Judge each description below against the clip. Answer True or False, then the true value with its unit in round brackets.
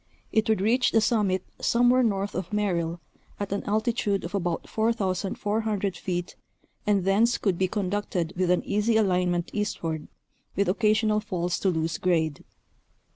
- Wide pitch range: False (3.2 semitones)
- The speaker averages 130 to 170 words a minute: True (150 wpm)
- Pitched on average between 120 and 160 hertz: False (200 Hz)